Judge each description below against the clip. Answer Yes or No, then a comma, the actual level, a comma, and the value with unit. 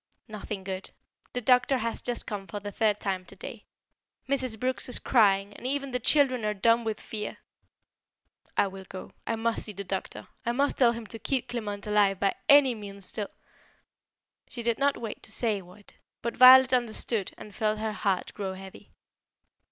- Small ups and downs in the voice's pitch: No, average, 3.6 semitones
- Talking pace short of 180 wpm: No, average, 185 wpm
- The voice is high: Yes, high, 220 Hz